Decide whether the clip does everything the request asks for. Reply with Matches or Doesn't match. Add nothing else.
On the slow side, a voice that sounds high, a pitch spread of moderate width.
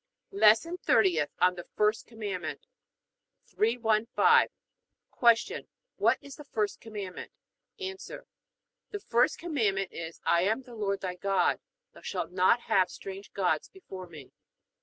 Matches